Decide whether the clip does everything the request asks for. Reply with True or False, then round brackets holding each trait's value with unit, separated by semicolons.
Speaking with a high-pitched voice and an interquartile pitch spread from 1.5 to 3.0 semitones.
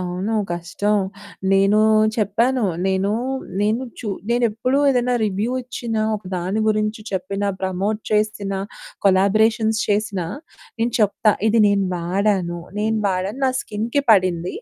True (210 Hz; 2.5 semitones)